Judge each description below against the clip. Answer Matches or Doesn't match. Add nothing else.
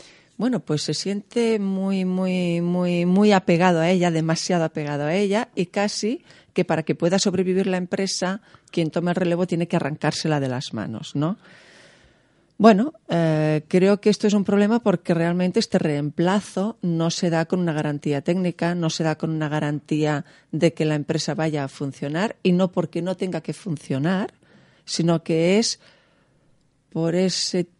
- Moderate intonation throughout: Matches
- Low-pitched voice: Doesn't match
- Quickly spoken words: Doesn't match